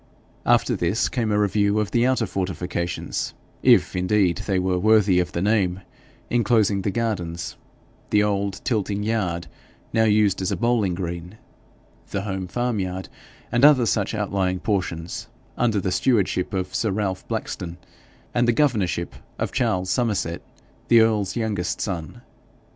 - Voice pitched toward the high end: No, low, 100 Hz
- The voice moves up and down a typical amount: Yes, average, 3.3 semitones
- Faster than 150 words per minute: No, average, 145 wpm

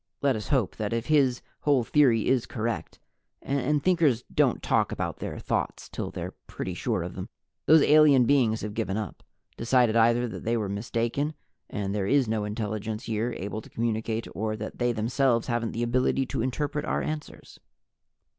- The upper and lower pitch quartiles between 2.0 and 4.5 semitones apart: Yes, average, 3.6 semitones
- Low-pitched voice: Yes, low, 115 Hz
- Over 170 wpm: Yes, average, 180 wpm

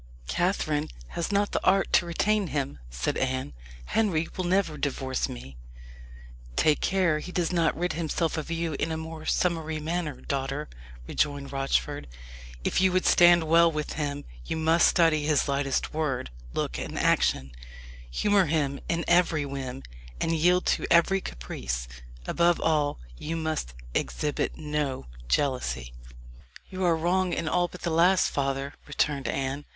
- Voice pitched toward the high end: No, medium, 155 Hz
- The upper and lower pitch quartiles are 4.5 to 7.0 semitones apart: No, average, 3.7 semitones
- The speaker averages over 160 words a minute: No, average, 155 wpm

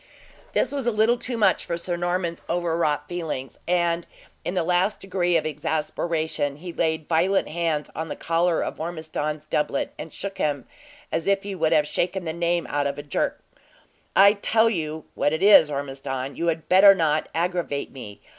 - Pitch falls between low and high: Yes, medium, 170 Hz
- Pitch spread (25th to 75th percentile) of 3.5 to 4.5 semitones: No, average, 3.0 semitones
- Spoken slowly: No, average, 185 wpm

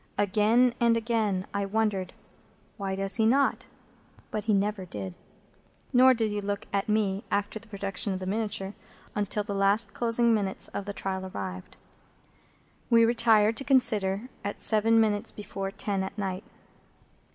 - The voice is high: Yes, high, 205 Hz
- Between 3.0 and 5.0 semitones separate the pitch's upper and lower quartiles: No, narrow, 2.4 semitones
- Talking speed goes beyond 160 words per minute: No, average, 155 wpm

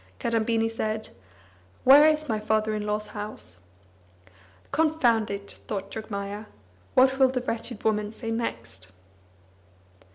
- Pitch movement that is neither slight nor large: No, narrow, 2.3 semitones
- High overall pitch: Yes, high, 220 Hz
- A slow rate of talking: Yes, slow, 120 wpm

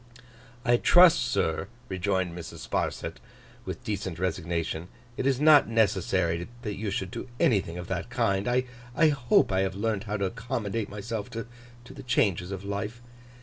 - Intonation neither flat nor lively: Yes, average, 4.4 semitones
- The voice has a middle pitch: No, low, 100 Hz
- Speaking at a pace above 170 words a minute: No, average, 155 wpm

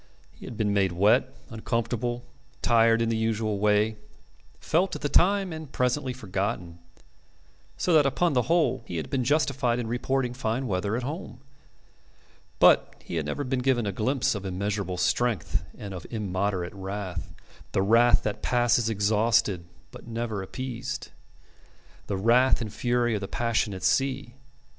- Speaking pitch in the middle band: No, low, 115 Hz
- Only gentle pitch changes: No, average, 3.8 semitones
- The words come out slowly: No, average, 155 wpm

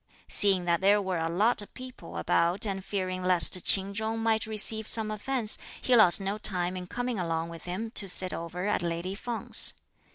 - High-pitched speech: Yes, high, 195 Hz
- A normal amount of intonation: Yes, average, 3.6 semitones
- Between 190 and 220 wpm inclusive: Yes, average, 195 wpm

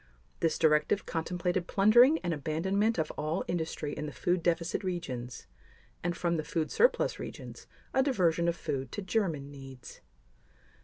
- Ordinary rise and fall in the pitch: Yes, average, 3.5 semitones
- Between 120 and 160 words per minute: Yes, average, 150 wpm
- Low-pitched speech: No, medium, 170 Hz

